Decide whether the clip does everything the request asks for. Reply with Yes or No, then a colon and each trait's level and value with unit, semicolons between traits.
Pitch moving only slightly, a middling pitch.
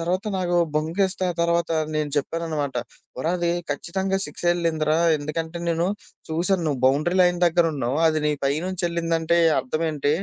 Yes: narrow, 2.2 semitones; medium, 165 Hz